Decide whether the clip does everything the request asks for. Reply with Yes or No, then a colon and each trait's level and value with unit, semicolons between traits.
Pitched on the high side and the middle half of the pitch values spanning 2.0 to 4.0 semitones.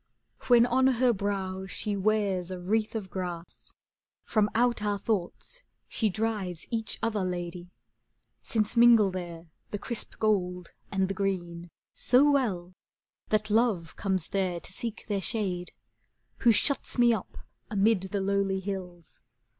Yes: high, 200 Hz; average, 3.5 semitones